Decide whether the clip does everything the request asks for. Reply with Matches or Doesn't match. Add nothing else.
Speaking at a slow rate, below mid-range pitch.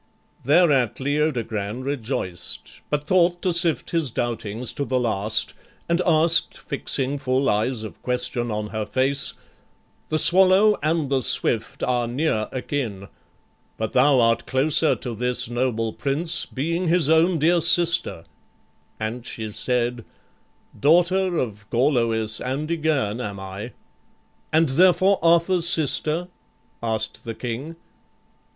Matches